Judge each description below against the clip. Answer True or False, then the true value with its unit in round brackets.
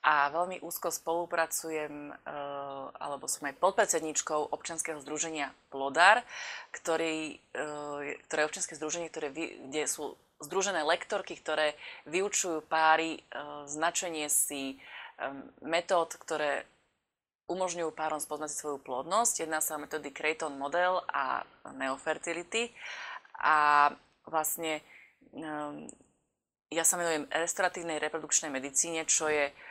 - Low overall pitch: False (155 Hz)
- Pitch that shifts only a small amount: True (2.3 semitones)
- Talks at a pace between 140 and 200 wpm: False (110 wpm)